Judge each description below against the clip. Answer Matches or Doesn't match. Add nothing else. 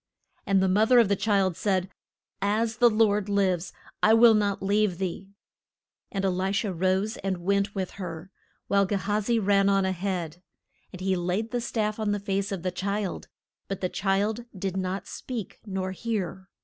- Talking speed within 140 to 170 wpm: Doesn't match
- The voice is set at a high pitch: Matches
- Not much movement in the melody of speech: Matches